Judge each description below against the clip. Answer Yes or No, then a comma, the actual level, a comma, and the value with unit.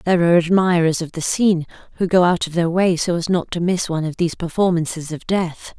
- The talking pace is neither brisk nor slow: No, fast, 240 wpm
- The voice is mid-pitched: Yes, medium, 170 Hz